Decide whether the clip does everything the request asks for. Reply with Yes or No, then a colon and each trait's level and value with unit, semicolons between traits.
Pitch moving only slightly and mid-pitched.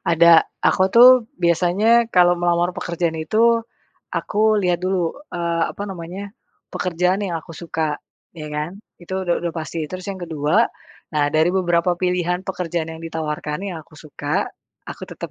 Yes: narrow, 1.8 semitones; medium, 170 Hz